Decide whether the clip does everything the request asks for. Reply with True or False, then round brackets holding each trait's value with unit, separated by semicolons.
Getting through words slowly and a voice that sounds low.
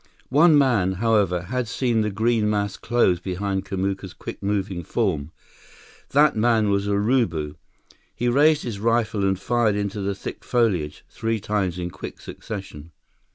False (150 wpm; 105 Hz)